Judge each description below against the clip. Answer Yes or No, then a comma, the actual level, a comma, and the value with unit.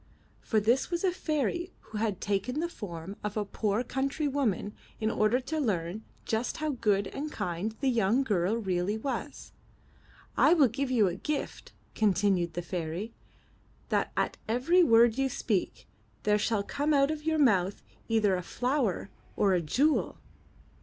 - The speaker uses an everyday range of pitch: No, wide, 5.7 semitones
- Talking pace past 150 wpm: Yes, average, 165 wpm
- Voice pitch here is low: No, high, 225 Hz